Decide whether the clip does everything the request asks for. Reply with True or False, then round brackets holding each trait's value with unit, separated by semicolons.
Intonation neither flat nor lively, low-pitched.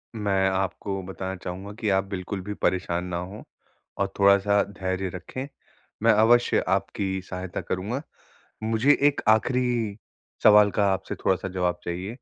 False (2.2 semitones; 95 Hz)